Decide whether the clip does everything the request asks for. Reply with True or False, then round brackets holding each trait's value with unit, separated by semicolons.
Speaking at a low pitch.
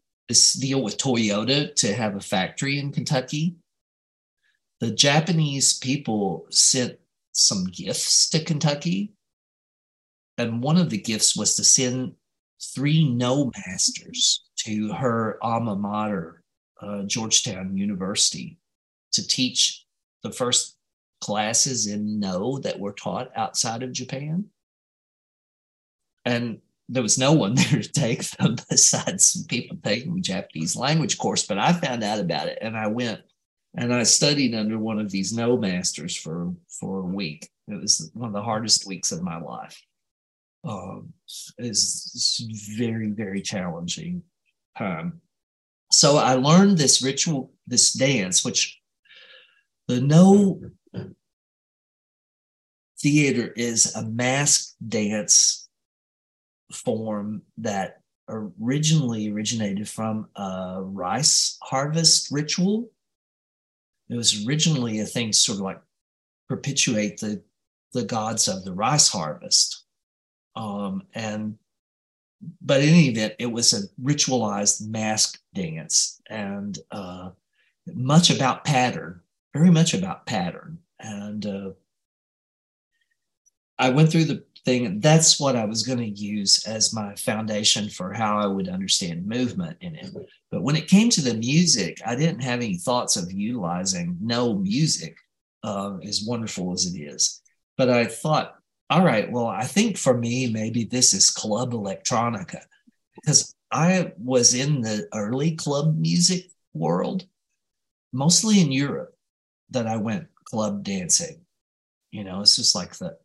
True (125 Hz)